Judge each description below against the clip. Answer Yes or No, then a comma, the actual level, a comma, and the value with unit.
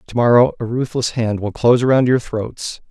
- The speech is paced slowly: No, fast, 205 wpm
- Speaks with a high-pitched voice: No, low, 120 Hz